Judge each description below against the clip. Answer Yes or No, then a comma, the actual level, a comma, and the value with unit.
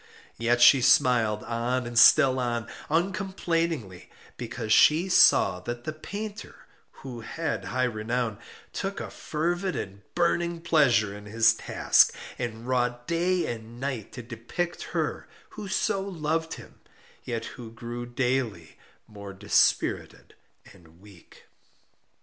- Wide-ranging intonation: Yes, wide, 6.4 semitones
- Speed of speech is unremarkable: No, slow, 125 wpm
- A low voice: Yes, low, 120 Hz